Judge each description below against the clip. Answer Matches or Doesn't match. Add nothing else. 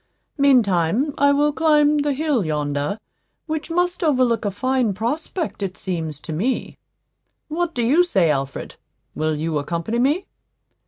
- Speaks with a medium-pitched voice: Doesn't match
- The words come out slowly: Doesn't match